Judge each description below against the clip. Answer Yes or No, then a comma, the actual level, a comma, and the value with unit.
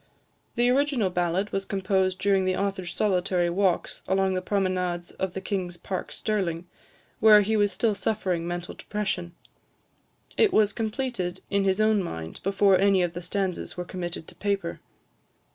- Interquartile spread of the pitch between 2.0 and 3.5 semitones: Yes, narrow, 2.5 semitones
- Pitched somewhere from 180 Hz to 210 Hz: Yes, high, 190 Hz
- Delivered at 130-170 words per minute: Yes, average, 160 wpm